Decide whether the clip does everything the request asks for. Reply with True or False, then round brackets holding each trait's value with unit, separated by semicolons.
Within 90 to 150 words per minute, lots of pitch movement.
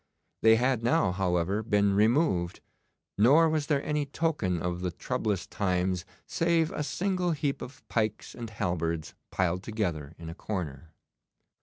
True (145 wpm; 7.7 semitones)